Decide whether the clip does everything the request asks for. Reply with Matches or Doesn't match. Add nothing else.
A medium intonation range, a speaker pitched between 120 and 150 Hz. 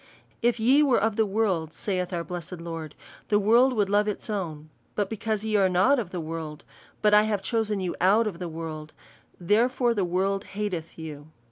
Doesn't match